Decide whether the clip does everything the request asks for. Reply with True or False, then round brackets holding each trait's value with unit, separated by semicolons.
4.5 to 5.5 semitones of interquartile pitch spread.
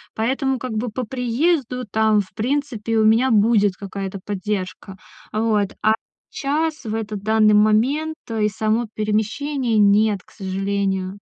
False (3.3 semitones)